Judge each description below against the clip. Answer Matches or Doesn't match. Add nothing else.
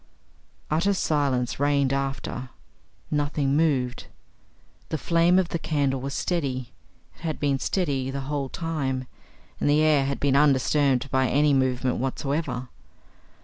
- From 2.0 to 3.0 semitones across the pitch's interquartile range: Matches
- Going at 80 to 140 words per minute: Matches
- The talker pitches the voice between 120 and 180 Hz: Matches